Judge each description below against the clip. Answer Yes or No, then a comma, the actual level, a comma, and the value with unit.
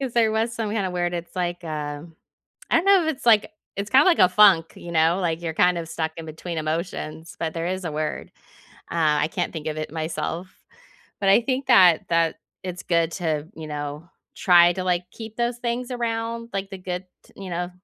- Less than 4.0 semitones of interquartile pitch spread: No, average, 5.1 semitones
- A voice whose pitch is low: No, medium, 175 Hz